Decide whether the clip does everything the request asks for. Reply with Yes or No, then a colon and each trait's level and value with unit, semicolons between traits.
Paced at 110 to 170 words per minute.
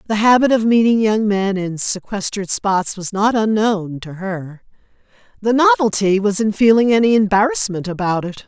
Yes: average, 165 wpm